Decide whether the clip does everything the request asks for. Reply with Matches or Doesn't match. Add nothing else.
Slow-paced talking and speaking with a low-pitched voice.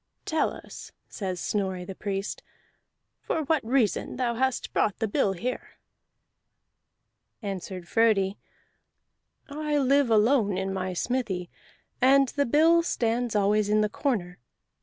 Doesn't match